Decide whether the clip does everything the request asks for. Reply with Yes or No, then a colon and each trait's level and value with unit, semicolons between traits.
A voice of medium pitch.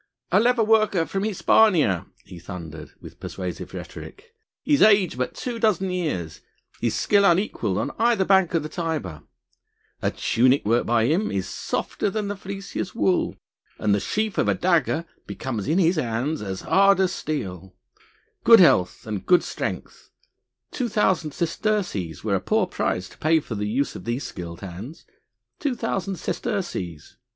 Yes: medium, 165 Hz